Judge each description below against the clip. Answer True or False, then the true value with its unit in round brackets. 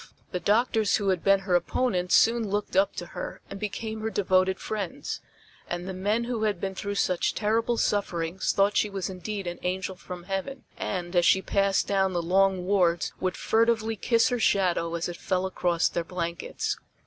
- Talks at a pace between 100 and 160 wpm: False (190 wpm)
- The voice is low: False (195 Hz)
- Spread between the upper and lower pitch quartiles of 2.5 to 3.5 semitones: True (2.8 semitones)